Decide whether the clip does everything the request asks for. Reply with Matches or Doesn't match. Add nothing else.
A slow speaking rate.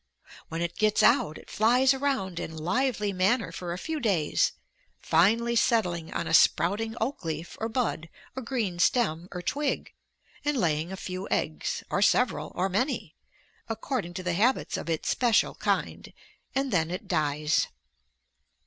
Doesn't match